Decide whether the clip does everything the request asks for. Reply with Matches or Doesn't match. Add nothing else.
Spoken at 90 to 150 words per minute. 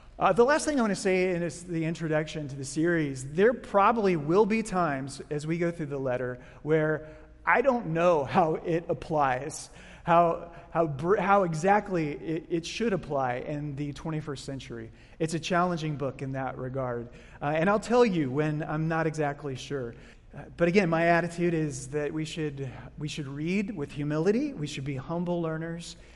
Doesn't match